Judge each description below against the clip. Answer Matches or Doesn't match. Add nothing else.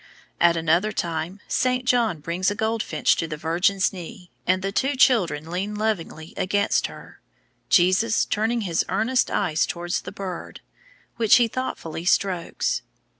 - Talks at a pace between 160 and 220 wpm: Doesn't match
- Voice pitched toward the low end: Doesn't match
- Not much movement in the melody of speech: Doesn't match